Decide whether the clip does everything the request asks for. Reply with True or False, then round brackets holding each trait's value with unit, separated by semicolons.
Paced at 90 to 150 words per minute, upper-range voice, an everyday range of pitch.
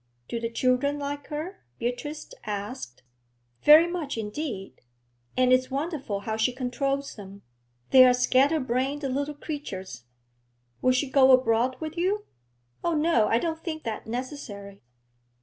True (140 wpm; 260 Hz; 4.4 semitones)